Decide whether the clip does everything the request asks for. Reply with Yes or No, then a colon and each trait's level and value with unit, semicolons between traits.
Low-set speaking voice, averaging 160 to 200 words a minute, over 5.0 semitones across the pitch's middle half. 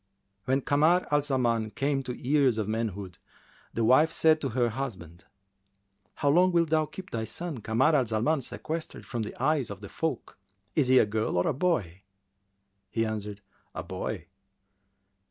Yes: low, 130 Hz; average, 170 wpm; wide, 5.6 semitones